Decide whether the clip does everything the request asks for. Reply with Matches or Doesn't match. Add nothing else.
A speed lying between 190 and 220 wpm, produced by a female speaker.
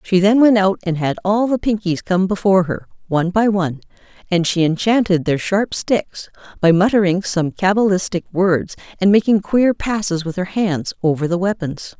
Doesn't match